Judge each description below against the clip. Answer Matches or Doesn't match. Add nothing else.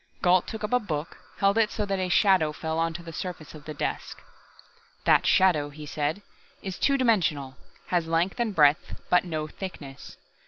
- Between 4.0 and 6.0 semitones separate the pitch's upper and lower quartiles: Matches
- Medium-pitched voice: Matches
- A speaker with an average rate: Matches